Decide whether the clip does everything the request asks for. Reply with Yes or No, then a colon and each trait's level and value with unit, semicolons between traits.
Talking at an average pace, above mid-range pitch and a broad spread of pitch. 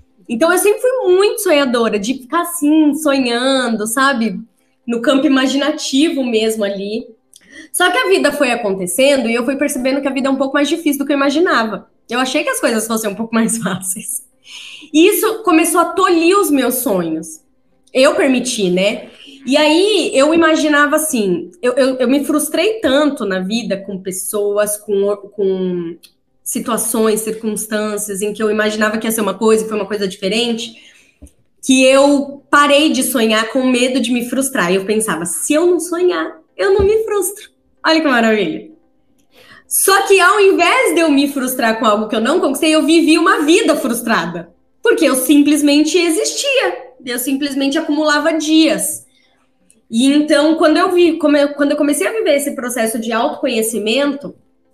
Yes: average, 170 wpm; very high, 270 Hz; wide, 5.9 semitones